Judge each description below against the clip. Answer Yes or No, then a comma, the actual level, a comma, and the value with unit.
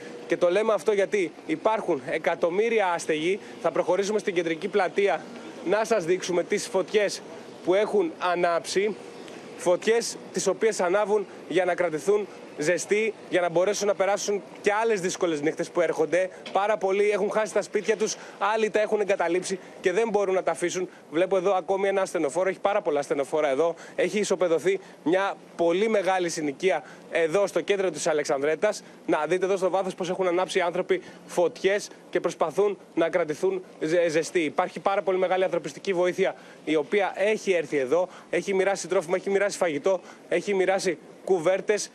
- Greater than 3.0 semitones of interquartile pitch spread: No, average, 2.7 semitones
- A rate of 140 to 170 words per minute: Yes, average, 165 wpm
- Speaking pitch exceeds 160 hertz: Yes, high, 190 Hz